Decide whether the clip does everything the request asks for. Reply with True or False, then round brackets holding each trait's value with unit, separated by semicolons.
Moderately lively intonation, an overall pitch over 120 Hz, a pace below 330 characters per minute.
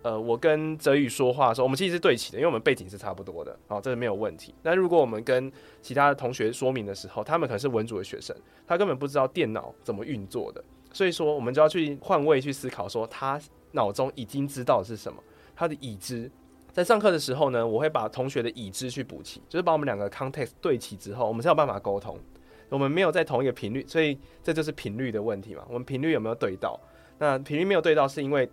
False (4.8 semitones; 135 Hz; 400 characters per minute)